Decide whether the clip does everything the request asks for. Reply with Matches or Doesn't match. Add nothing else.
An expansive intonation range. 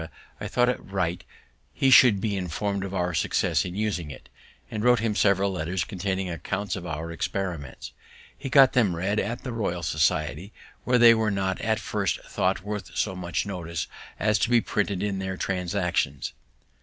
Doesn't match